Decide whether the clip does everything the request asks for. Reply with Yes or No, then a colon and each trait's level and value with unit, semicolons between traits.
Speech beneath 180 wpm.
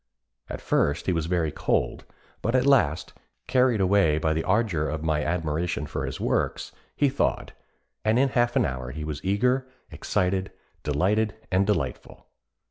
Yes: average, 160 wpm